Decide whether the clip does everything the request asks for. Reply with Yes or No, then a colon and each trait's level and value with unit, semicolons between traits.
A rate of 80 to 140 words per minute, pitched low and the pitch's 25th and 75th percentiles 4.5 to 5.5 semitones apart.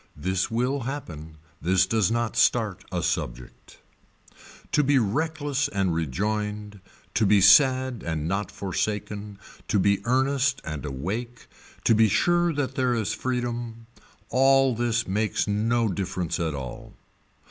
Yes: slow, 135 wpm; low, 110 Hz; average, 5.2 semitones